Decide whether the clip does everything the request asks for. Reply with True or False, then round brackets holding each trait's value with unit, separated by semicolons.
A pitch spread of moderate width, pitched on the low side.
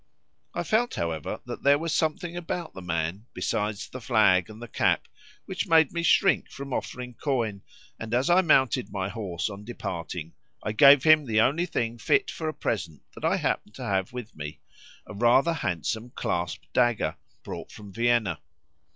False (6.7 semitones; 115 Hz)